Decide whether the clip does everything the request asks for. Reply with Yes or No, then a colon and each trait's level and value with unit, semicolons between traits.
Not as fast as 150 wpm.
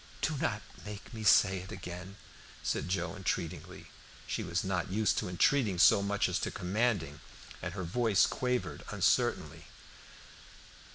Yes: average, 140 wpm